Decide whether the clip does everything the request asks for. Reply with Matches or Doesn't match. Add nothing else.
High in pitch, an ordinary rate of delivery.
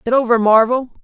Matches